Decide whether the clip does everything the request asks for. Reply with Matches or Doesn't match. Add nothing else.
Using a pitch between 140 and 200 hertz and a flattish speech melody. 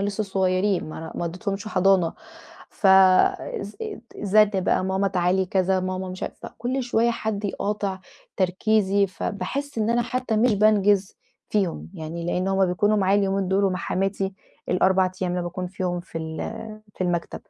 Matches